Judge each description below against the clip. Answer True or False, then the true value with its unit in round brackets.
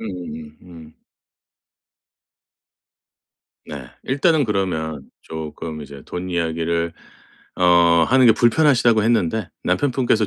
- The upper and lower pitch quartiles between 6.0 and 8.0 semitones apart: True (6.5 semitones)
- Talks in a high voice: False (90 Hz)